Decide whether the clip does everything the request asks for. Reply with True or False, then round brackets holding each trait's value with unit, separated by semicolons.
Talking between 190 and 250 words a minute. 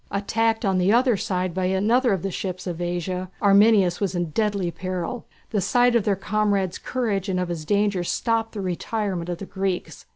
True (195 wpm)